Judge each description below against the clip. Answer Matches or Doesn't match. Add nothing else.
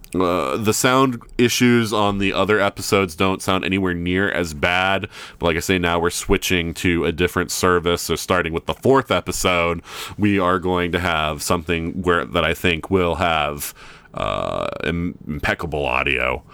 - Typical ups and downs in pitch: Doesn't match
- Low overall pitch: Matches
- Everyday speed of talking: Matches